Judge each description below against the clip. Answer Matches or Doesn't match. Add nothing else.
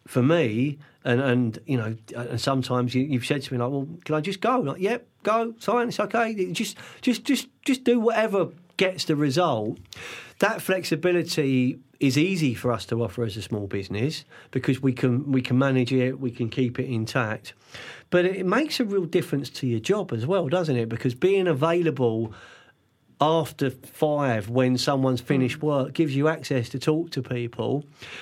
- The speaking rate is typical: Matches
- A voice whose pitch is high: Doesn't match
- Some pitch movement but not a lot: Doesn't match